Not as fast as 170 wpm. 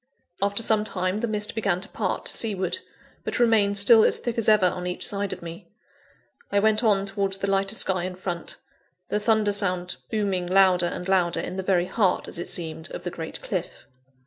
No: fast, 205 wpm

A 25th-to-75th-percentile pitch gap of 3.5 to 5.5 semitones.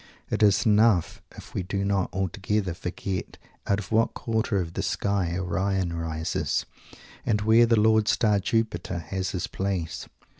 No: average, 2.9 semitones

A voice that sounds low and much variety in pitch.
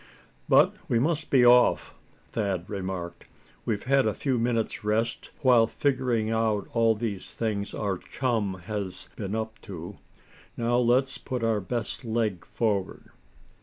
No: low, 110 Hz; average, 3.1 semitones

